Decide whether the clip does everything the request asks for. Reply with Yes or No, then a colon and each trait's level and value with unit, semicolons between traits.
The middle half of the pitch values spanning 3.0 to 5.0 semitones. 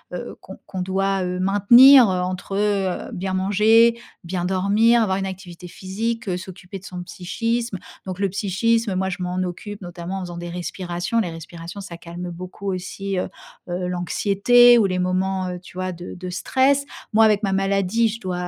No: narrow, 2.4 semitones